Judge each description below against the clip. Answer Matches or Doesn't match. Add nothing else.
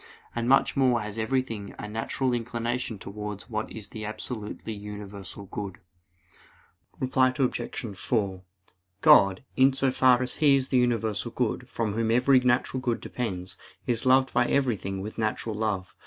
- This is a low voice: Matches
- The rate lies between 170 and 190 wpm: Doesn't match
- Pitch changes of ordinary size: Matches